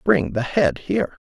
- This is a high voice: No, medium, 160 Hz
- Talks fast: No, average, 190 wpm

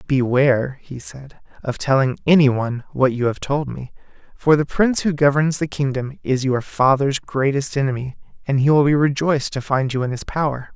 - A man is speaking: Yes, male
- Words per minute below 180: No, average, 195 wpm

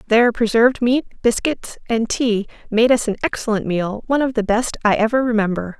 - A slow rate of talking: No, average, 185 wpm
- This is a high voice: Yes, high, 230 Hz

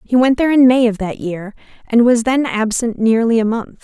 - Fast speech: Yes, fast, 235 wpm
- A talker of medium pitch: No, high, 230 Hz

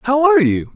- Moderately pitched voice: No, very high, 290 Hz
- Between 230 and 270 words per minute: Yes, fast, 240 wpm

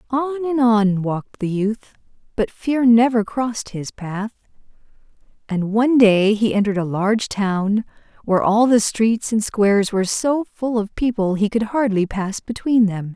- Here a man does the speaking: No, female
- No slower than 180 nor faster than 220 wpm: No, average, 170 wpm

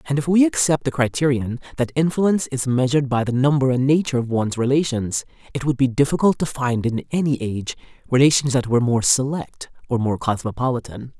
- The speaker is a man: No, female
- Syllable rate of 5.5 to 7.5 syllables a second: Yes, 6.0 syllables/s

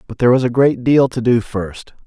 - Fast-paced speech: Yes, fast, 260 wpm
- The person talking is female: No, male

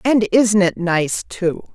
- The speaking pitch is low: No, high, 195 Hz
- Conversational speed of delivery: Yes, average, 170 wpm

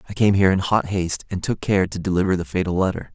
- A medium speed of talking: No, fast, 265 wpm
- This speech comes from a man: Yes, male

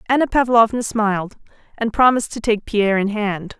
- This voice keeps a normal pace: Yes, average, 165 wpm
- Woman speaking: Yes, female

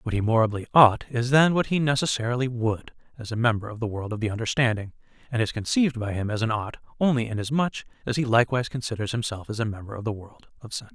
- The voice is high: No, low, 115 Hz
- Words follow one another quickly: Yes, fast, 230 wpm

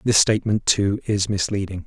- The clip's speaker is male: Yes, male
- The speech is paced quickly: No, average, 160 wpm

